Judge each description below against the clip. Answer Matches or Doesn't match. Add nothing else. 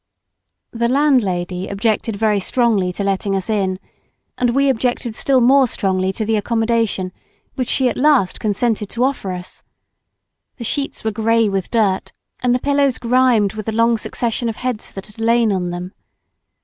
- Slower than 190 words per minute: Matches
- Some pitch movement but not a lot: Matches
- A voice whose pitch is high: Matches